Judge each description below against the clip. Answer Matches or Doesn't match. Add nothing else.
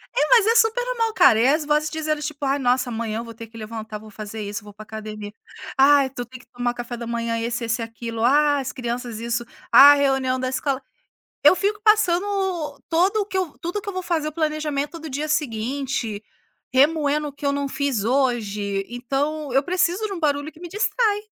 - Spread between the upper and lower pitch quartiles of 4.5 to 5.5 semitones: Matches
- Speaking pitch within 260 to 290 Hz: Matches